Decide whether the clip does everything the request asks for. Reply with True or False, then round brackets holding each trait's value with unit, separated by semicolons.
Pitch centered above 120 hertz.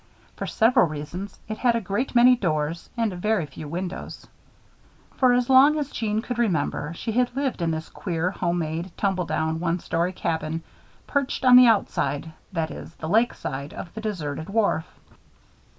True (185 Hz)